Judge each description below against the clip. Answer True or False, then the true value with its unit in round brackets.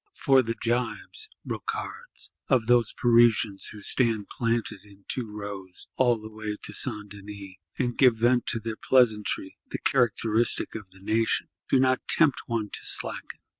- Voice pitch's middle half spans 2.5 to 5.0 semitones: True (2.8 semitones)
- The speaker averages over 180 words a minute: False (160 wpm)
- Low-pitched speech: True (115 Hz)